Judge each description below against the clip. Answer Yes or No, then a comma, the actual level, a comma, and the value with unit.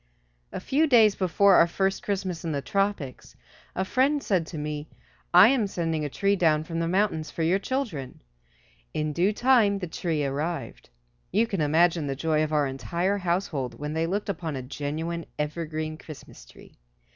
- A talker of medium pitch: Yes, medium, 170 Hz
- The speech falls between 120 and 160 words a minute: No, average, 180 wpm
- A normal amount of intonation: Yes, average, 4.5 semitones